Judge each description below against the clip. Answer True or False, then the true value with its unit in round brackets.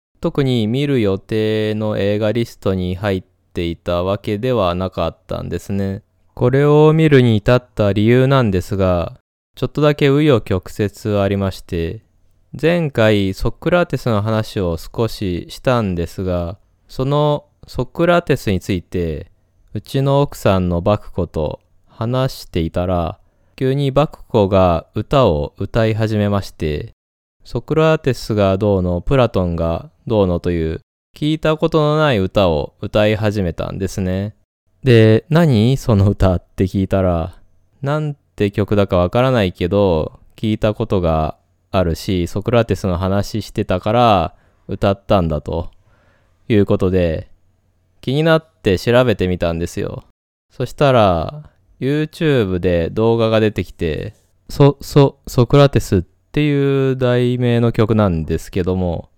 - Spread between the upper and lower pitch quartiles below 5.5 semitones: True (5.1 semitones)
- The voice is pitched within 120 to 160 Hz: False (105 Hz)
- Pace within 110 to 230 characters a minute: False (280 characters per minute)